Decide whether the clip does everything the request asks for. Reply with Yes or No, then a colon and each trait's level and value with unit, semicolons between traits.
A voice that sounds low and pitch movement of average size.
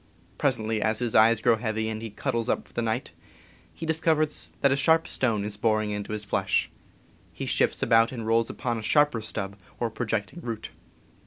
Yes: low, 115 Hz; average, 3.0 semitones